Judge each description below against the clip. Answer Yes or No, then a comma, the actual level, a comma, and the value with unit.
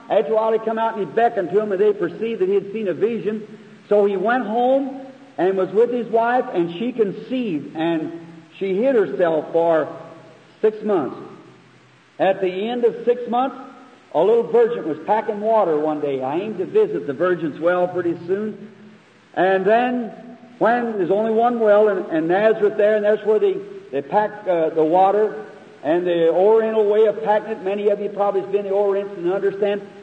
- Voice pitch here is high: Yes, high, 210 Hz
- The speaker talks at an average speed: Yes, average, 190 wpm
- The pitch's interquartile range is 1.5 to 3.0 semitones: No, average, 3.5 semitones